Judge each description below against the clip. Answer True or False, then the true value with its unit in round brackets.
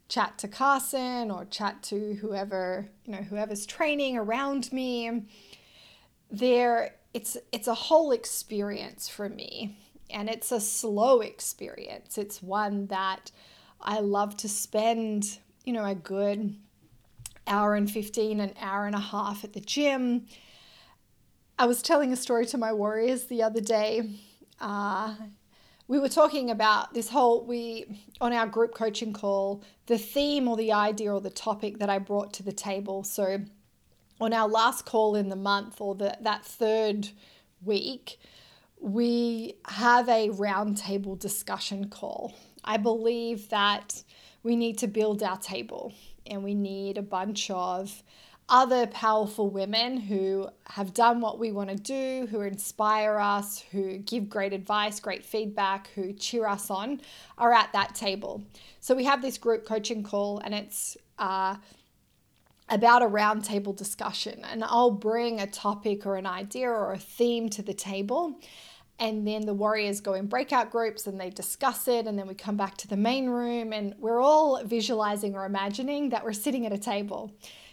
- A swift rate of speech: False (160 wpm)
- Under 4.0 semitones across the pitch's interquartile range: True (2.7 semitones)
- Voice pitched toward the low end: False (215 Hz)